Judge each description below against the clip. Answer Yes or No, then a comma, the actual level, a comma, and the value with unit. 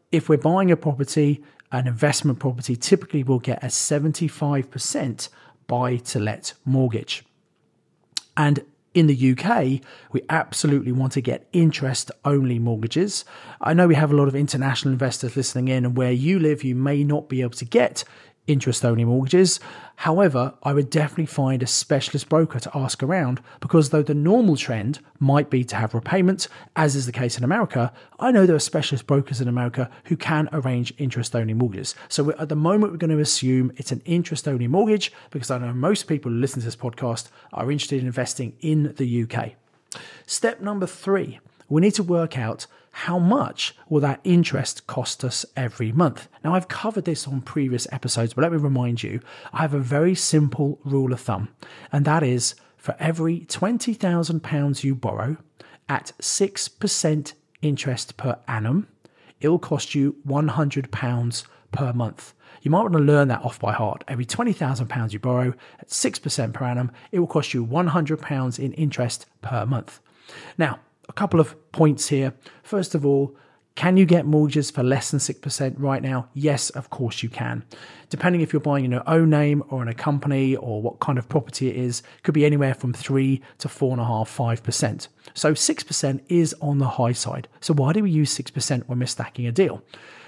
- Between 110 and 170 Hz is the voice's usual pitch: Yes, medium, 140 Hz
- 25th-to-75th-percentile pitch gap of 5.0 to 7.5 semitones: No, average, 3.7 semitones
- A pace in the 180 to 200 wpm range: Yes, average, 185 wpm